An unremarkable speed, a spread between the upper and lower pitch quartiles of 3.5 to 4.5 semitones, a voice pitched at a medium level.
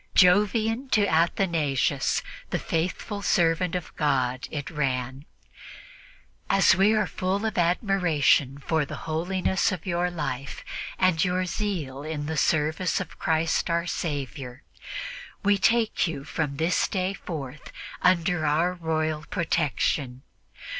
No: slow, 125 wpm; average, 3.9 semitones; medium, 165 Hz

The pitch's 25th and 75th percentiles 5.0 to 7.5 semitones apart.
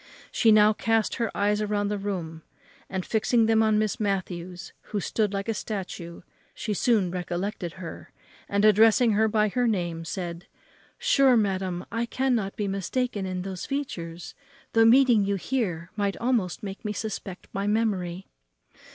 No: average, 3.2 semitones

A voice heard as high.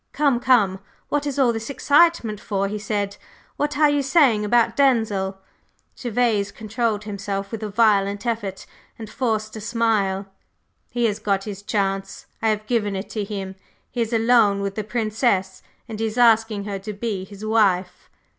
Yes: high, 215 Hz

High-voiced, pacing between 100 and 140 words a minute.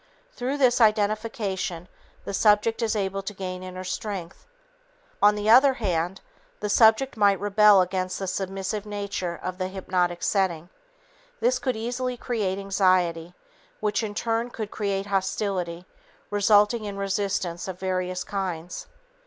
Yes: high, 200 Hz; slow, 135 wpm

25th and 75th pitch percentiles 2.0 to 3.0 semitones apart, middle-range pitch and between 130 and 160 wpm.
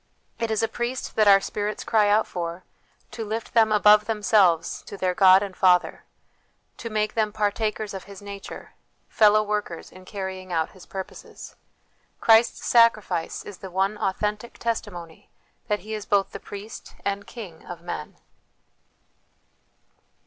No: narrow, 2.4 semitones; high, 205 Hz; average, 150 wpm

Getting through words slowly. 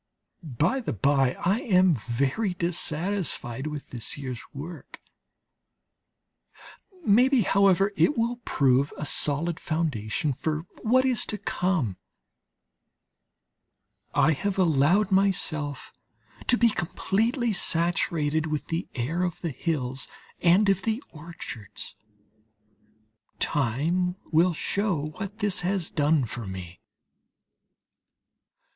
Yes: slow, 105 wpm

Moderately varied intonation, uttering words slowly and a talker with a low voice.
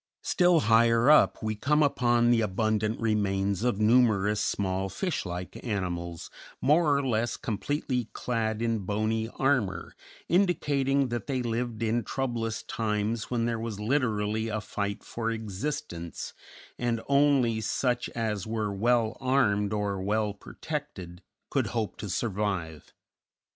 Yes: average, 3.2 semitones; slow, 130 wpm; low, 115 Hz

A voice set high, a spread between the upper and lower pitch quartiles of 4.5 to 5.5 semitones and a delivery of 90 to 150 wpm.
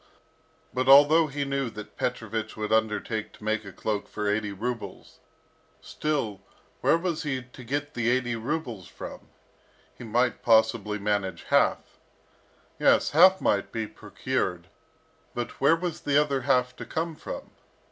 No: low, 120 Hz; average, 4.8 semitones; average, 145 wpm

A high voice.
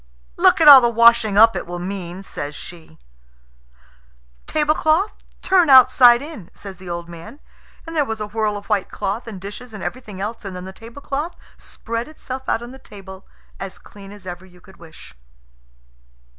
Yes: high, 215 Hz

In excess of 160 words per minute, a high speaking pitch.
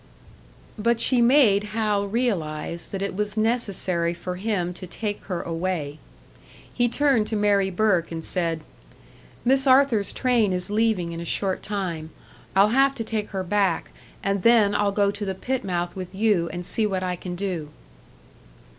Yes: average, 170 wpm; high, 200 Hz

